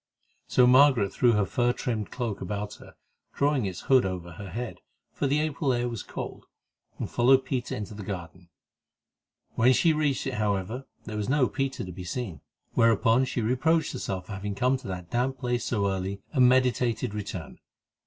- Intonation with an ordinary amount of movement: Yes, average, 4.7 semitones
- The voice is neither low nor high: No, low, 120 Hz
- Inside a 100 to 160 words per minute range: No, average, 185 wpm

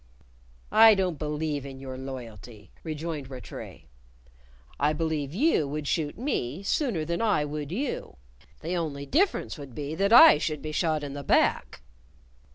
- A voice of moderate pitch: Yes, medium, 150 Hz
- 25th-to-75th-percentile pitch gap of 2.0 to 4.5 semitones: Yes, average, 3.6 semitones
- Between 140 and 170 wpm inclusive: Yes, average, 155 wpm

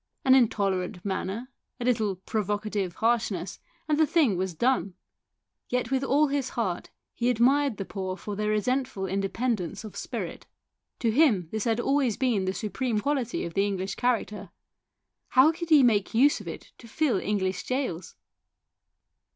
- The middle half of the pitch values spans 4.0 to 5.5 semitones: Yes, average, 4.9 semitones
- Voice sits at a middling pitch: No, high, 220 Hz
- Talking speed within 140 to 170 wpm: Yes, average, 160 wpm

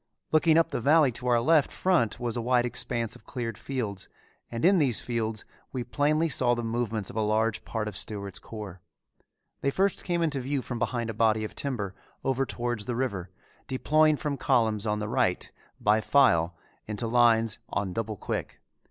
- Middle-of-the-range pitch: No, low, 120 Hz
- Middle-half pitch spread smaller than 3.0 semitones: No, average, 3.8 semitones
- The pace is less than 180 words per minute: No, average, 185 wpm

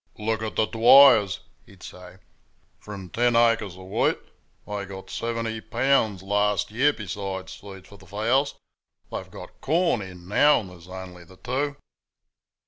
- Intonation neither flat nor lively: Yes, average, 3.7 semitones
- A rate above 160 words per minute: No, average, 150 wpm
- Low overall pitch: Yes, low, 105 Hz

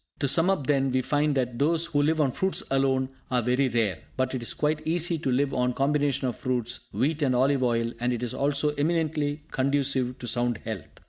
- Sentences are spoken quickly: Yes, fast, 220 wpm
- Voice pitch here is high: No, low, 135 Hz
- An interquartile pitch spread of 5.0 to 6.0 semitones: No, average, 2.9 semitones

